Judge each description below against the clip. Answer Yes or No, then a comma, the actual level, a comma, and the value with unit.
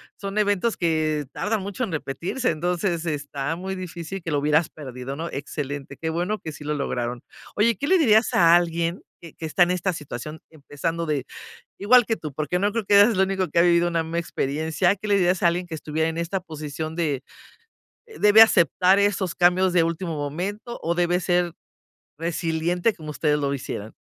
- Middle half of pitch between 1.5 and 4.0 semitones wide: Yes, average, 3.7 semitones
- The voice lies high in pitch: No, medium, 170 Hz